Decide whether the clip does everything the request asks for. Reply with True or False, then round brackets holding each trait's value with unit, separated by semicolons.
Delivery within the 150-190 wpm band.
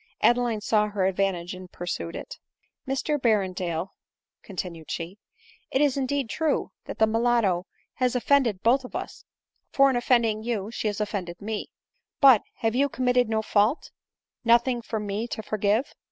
True (165 wpm)